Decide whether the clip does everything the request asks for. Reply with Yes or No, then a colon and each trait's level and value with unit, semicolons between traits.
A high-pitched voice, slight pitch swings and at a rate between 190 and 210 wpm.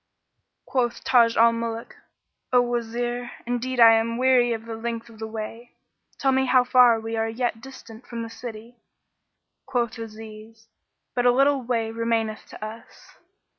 No: high, 230 Hz; narrow, 1.6 semitones; average, 160 wpm